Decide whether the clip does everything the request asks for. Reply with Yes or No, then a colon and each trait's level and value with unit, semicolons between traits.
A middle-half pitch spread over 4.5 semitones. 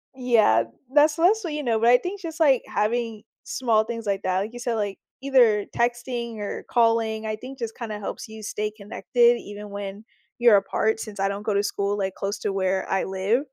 No: average, 3.0 semitones